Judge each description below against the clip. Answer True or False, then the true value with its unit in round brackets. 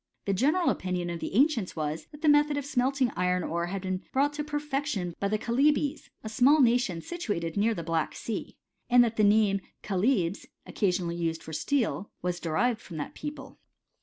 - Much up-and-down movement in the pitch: True (7.6 semitones)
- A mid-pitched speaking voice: False (215 Hz)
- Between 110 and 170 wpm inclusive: False (195 wpm)